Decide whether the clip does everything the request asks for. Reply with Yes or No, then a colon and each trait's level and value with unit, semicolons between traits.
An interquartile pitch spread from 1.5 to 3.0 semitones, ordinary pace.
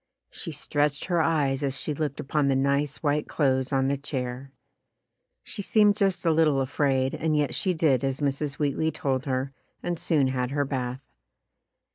Yes: narrow, 2.5 semitones; average, 175 wpm